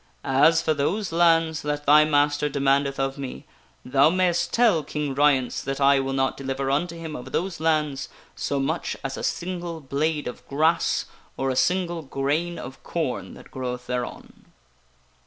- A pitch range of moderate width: Yes, average, 3.3 semitones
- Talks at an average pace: Yes, average, 165 wpm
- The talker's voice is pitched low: No, medium, 145 Hz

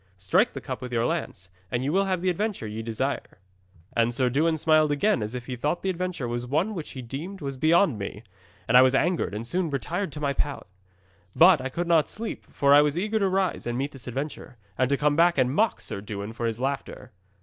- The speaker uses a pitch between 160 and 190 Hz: No, medium, 140 Hz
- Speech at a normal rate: No, fast, 240 wpm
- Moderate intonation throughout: No, wide, 5.8 semitones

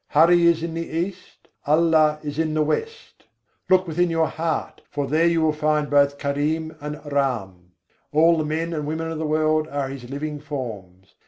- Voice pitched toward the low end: No, medium, 155 Hz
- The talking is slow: No, average, 185 wpm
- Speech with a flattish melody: Yes, narrow, 2.2 semitones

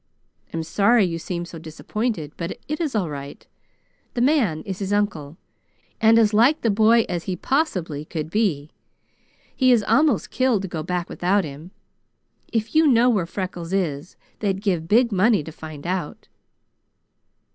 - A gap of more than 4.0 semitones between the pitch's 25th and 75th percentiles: Yes, wide, 5.5 semitones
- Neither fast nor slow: Yes, average, 165 wpm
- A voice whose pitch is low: No, high, 190 Hz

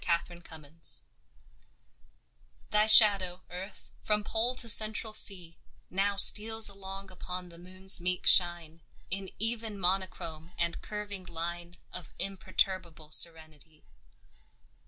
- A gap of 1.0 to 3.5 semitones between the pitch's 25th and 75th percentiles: Yes, average, 3.1 semitones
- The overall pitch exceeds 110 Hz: Yes, medium, 185 Hz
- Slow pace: Yes, slow, 115 wpm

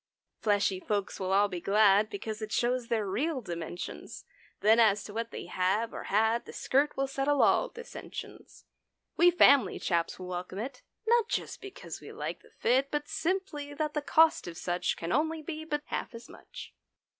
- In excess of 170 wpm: Yes, average, 185 wpm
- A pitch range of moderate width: No, wide, 6.8 semitones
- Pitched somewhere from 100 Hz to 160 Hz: No, high, 230 Hz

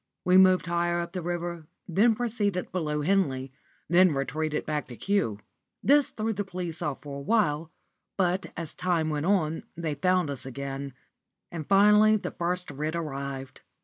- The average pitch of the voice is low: No, medium, 170 Hz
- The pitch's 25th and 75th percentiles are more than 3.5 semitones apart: Yes, average, 4.2 semitones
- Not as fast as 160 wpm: No, average, 165 wpm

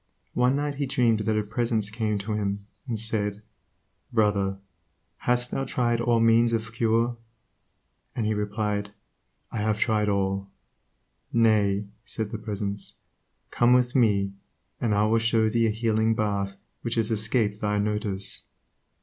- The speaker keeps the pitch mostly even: Yes, narrow, 2.1 semitones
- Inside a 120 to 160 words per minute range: Yes, average, 150 wpm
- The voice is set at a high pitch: No, low, 110 Hz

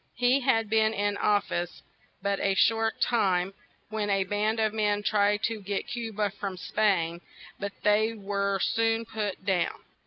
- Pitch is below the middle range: No, high, 205 Hz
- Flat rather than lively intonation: Yes, narrow, 1.9 semitones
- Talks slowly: No, average, 165 wpm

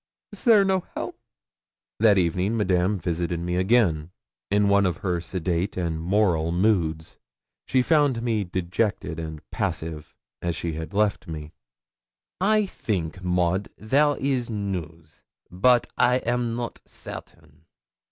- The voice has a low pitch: Yes, very low, 95 Hz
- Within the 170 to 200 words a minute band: No, slow, 135 wpm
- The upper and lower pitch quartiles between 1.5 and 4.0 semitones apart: No, average, 5.3 semitones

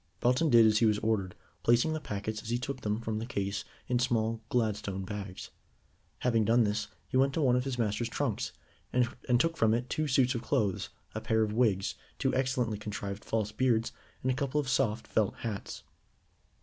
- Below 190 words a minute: No, average, 200 wpm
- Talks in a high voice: No, low, 115 Hz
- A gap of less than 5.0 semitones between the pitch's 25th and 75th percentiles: Yes, average, 3.0 semitones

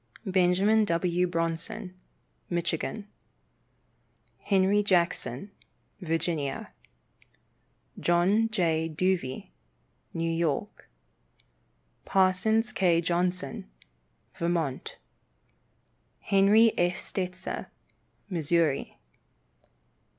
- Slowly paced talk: Yes, slow, 60 wpm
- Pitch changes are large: No, average, 2.7 semitones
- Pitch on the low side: No, medium, 180 Hz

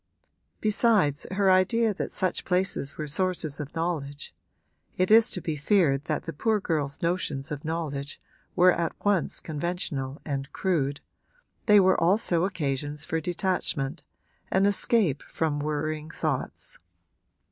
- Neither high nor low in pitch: Yes, medium, 165 Hz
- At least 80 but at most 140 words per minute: Yes, slow, 135 wpm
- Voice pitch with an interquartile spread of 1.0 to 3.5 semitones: No, average, 4.3 semitones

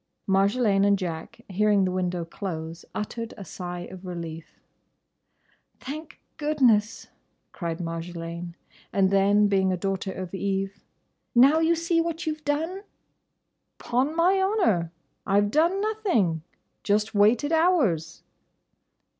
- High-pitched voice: Yes, high, 200 Hz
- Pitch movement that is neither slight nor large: No, wide, 8.9 semitones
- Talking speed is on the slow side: Yes, slow, 125 wpm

